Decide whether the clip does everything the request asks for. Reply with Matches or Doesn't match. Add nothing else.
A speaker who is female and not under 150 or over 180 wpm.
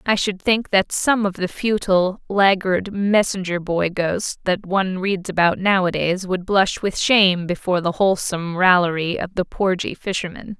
Matches